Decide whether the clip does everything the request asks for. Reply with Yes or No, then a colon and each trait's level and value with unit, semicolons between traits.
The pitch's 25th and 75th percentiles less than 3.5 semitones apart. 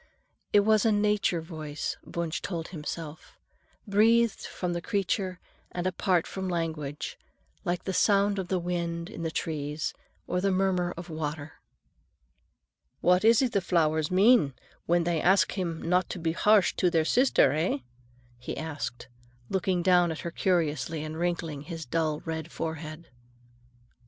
Yes: average, 3.0 semitones